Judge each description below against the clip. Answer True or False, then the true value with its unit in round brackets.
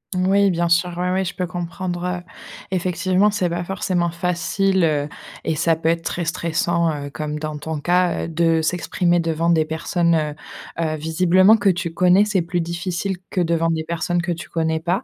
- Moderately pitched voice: True (170 Hz)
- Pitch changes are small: True (1.9 semitones)